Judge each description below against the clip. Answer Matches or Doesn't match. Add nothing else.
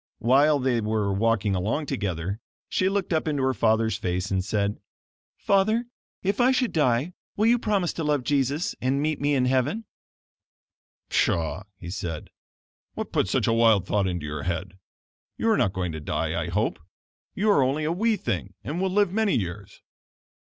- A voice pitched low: Matches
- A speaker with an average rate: Matches